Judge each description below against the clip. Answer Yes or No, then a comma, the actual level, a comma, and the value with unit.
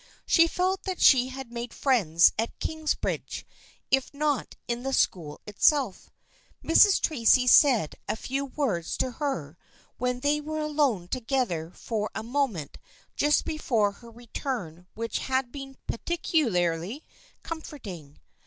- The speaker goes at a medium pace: No, slow, 130 wpm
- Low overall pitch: No, very high, 250 Hz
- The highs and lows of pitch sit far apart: Yes, wide, 5.7 semitones